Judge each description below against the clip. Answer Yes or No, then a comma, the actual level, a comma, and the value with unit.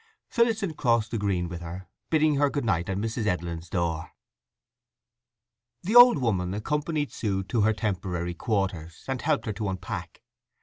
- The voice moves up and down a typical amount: No, wide, 7.8 semitones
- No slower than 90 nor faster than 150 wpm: No, average, 160 wpm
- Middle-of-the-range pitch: No, low, 105 Hz